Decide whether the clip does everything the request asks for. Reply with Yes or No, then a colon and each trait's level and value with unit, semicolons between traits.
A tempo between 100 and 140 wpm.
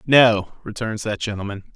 Yes: slow, 135 wpm